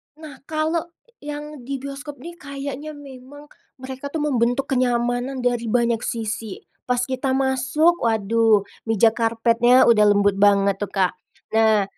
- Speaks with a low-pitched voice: No, very high, 250 Hz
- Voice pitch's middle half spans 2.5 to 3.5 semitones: No, average, 3.9 semitones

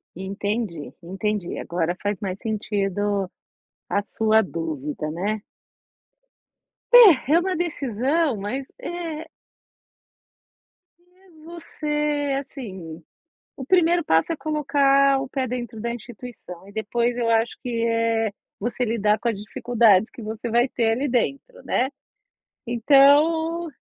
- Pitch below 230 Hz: No, high, 235 Hz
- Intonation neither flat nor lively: No, wide, 5.7 semitones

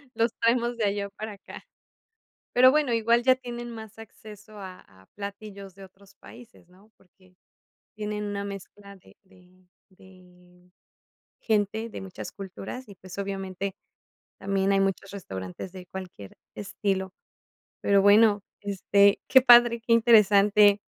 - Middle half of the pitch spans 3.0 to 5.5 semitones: No, narrow, 2.5 semitones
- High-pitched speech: Yes, high, 200 Hz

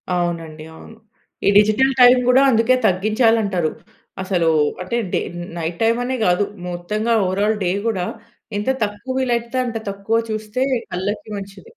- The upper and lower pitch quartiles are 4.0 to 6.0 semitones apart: Yes, average, 4.4 semitones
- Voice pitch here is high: Yes, high, 210 Hz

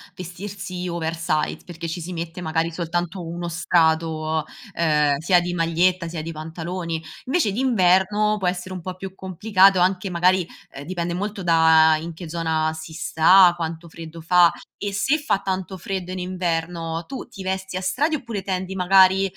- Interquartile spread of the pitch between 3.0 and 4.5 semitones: No, narrow, 2.5 semitones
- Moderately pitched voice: Yes, medium, 175 Hz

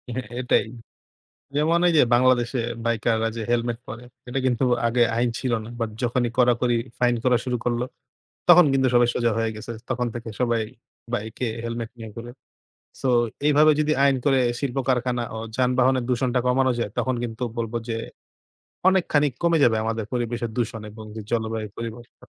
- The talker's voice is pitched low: Yes, low, 120 Hz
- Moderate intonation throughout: No, narrow, 1.8 semitones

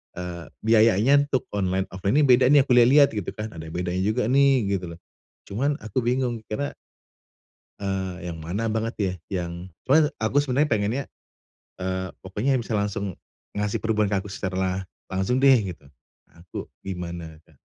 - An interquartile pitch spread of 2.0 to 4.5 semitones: No, average, 5.1 semitones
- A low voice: Yes, low, 105 Hz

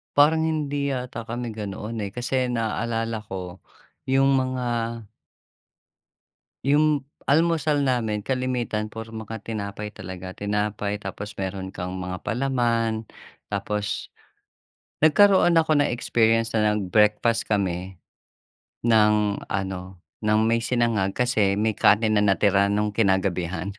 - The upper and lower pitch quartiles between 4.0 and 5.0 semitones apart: No, average, 3.6 semitones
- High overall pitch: No, low, 110 Hz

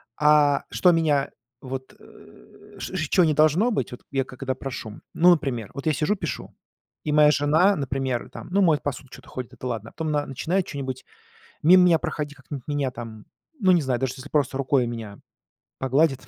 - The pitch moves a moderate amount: Yes, average, 3.3 semitones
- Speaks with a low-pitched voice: No, medium, 145 Hz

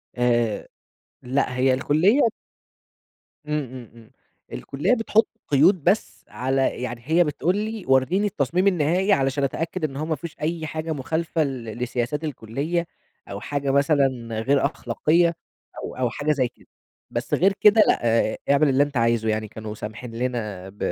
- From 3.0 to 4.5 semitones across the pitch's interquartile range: No, average, 5.1 semitones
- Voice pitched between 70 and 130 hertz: No, medium, 140 Hz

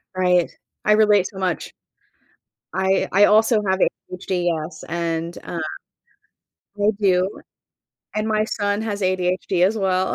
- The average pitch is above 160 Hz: Yes, high, 190 Hz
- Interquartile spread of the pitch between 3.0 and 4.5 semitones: No, narrow, 2.5 semitones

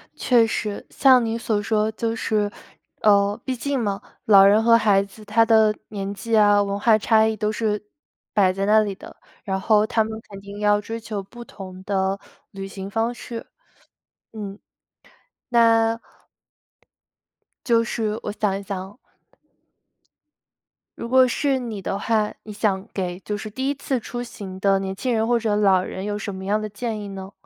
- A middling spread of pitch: No, narrow, 2.3 semitones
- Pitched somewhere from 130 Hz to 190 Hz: No, high, 210 Hz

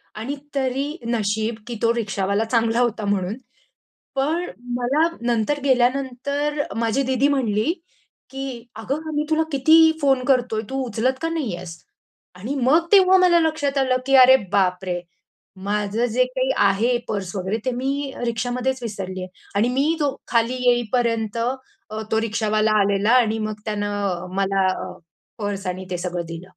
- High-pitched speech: Yes, high, 235 Hz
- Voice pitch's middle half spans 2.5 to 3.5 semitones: No, average, 4.6 semitones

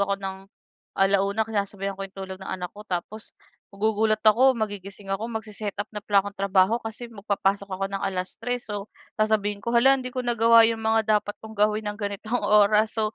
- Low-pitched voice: No, high, 210 Hz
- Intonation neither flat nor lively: No, narrow, 1.9 semitones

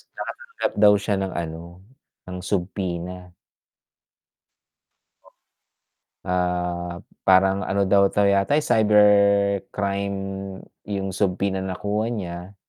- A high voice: No, very low, 95 Hz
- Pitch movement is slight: Yes, narrow, 2.0 semitones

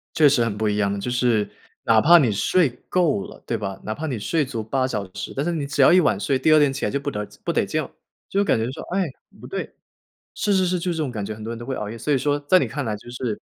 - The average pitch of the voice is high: No, low, 130 Hz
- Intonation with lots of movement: Yes, wide, 6.1 semitones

